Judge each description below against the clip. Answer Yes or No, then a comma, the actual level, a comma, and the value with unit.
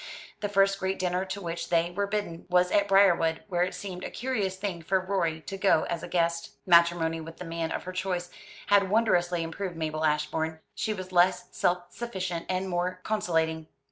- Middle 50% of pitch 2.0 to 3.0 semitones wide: Yes, narrow, 2.6 semitones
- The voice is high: No, medium, 180 Hz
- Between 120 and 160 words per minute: No, average, 195 wpm